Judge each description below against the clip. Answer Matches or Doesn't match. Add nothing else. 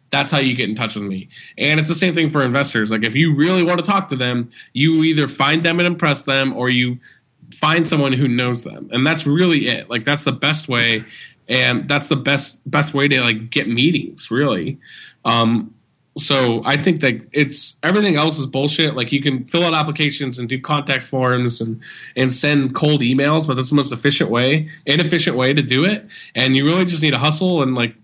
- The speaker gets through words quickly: Matches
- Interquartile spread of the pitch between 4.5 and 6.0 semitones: Doesn't match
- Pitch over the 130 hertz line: Matches